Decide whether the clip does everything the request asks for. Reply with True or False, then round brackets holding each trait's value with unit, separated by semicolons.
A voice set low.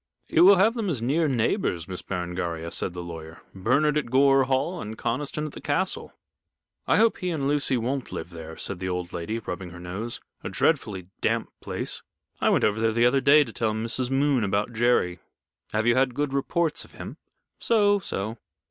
True (120 Hz)